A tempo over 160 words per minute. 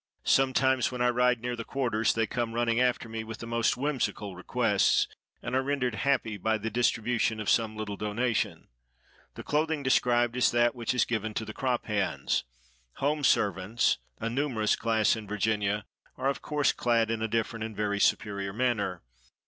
Yes: average, 180 wpm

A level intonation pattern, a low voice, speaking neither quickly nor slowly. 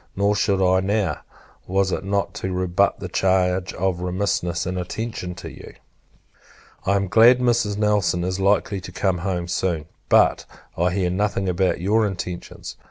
Yes: narrow, 1.9 semitones; very low, 95 Hz; average, 165 wpm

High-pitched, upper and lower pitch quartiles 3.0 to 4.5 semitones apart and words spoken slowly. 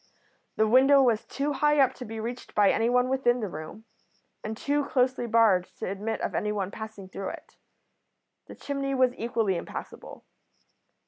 No: high, 230 Hz; average, 3.7 semitones; average, 165 wpm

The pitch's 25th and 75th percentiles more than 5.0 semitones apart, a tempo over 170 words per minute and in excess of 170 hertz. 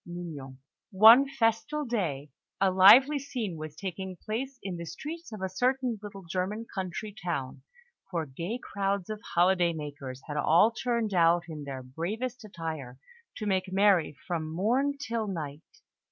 No: wide, 5.5 semitones; average, 155 wpm; high, 190 Hz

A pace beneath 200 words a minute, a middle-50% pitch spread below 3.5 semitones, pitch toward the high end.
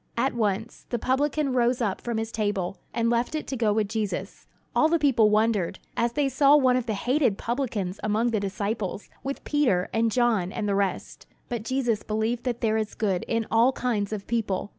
No: fast, 205 wpm; average, 3.1 semitones; high, 230 Hz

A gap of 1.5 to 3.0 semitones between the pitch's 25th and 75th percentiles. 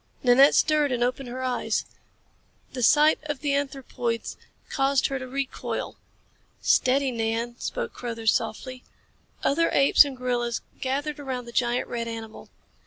Yes: narrow, 2.6 semitones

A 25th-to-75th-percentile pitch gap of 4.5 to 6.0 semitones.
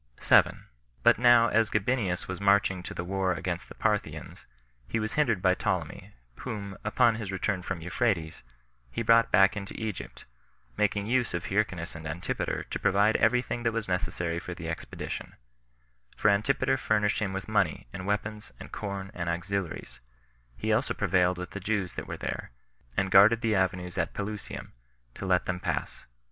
No: average, 3.2 semitones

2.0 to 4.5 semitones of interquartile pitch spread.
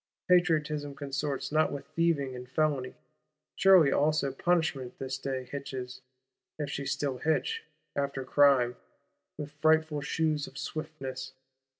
Yes: average, 2.7 semitones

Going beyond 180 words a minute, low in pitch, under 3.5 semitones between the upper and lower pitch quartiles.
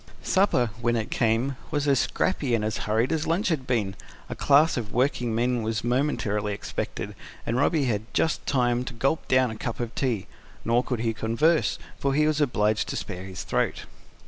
No: average, 195 wpm; low, 120 Hz; average, 4.1 semitones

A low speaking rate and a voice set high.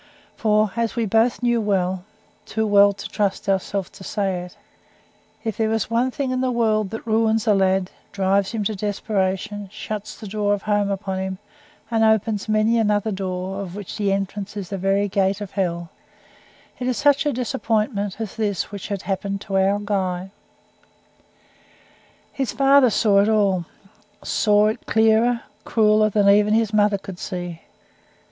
No: average, 170 wpm; high, 205 Hz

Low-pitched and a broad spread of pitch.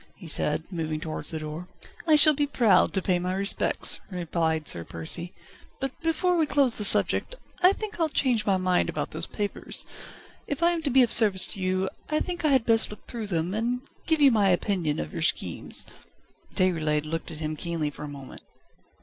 No: high, 195 Hz; wide, 8.8 semitones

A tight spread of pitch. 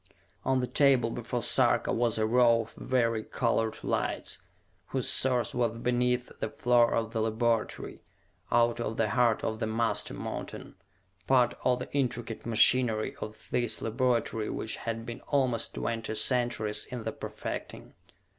Yes: narrow, 1.6 semitones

